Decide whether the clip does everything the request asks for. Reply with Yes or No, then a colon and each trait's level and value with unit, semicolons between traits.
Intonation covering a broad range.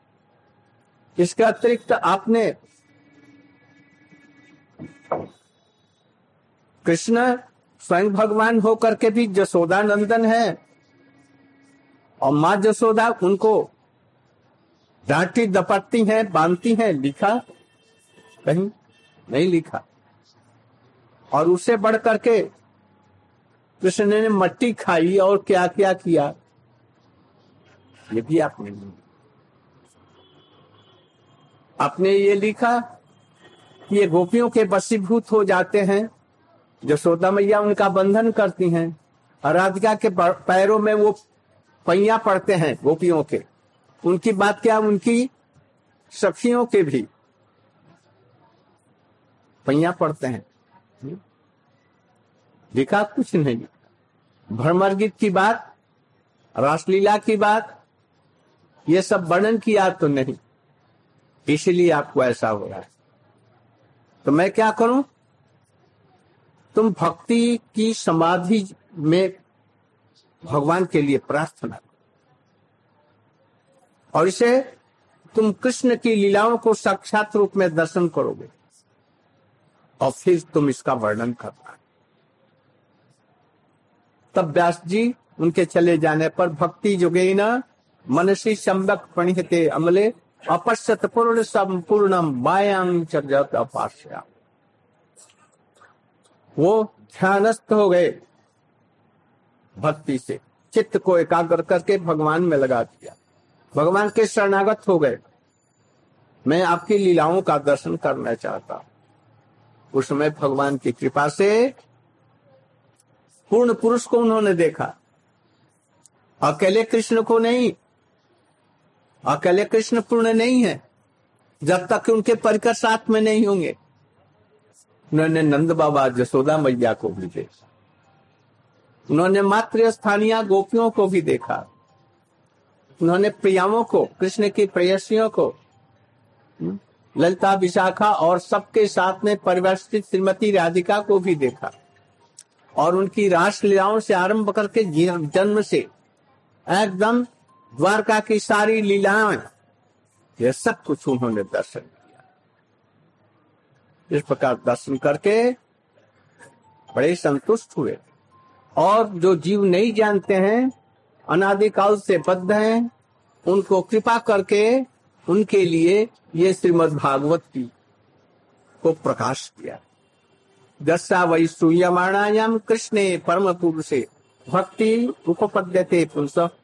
Yes: wide, 6.2 semitones